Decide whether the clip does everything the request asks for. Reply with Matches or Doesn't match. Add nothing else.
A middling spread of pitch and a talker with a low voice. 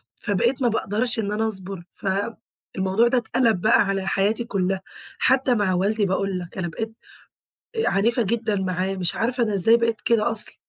Doesn't match